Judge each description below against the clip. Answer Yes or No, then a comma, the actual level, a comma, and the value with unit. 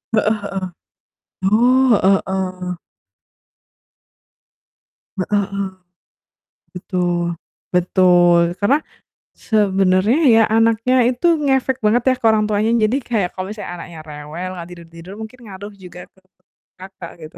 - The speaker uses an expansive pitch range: No, average, 3.4 semitones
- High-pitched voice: Yes, high, 195 Hz